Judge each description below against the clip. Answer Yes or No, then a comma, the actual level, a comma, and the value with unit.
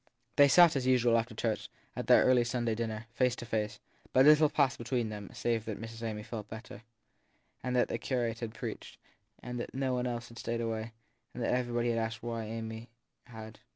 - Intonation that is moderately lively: No, narrow, 1.8 semitones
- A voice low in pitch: Yes, low, 115 Hz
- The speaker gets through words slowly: No, average, 190 wpm